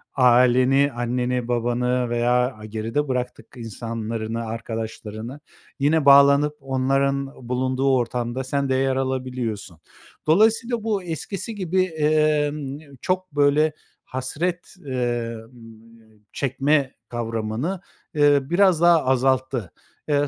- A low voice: Yes, low, 130 Hz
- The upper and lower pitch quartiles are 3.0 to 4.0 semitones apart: Yes, average, 3.7 semitones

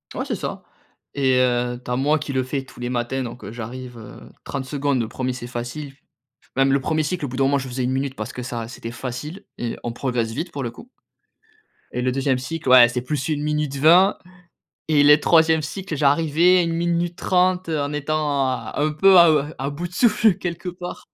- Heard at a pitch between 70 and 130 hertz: No, medium, 140 Hz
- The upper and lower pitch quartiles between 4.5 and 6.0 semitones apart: No, average, 4.1 semitones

